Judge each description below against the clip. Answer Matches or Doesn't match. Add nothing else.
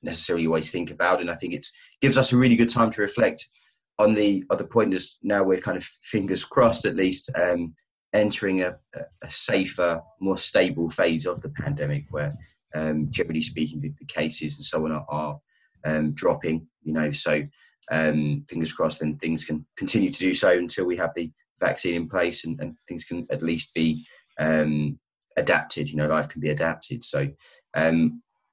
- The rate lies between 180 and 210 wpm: Matches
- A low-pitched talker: Matches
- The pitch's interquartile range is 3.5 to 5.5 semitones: Doesn't match